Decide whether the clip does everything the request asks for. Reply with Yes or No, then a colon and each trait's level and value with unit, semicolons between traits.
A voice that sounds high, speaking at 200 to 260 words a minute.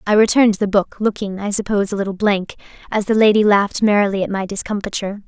Yes: high, 205 Hz; fast, 205 wpm